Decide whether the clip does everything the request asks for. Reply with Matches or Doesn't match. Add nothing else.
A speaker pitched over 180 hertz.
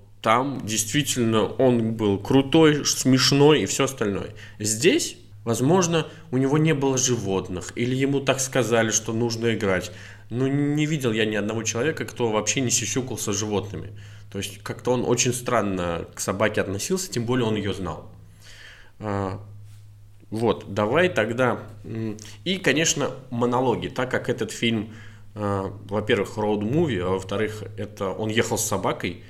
Doesn't match